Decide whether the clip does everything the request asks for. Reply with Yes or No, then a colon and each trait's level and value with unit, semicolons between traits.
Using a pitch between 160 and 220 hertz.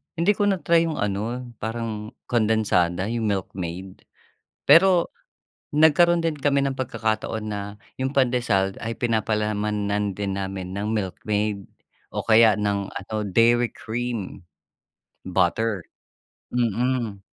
No: low, 110 Hz